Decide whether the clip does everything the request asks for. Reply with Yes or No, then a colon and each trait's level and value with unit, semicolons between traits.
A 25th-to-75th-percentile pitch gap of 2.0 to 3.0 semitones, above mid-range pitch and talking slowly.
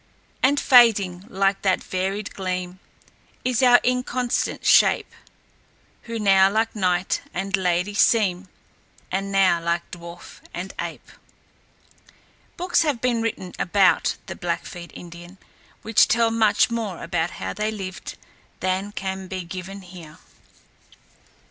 No: average, 3.6 semitones; high, 195 Hz; slow, 125 wpm